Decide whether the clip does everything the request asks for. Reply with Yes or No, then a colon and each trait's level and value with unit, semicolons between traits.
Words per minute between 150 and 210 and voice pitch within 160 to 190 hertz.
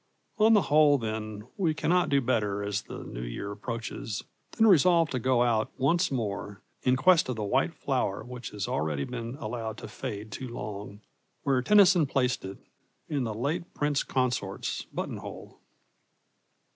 No: average, 160 wpm; low, 125 Hz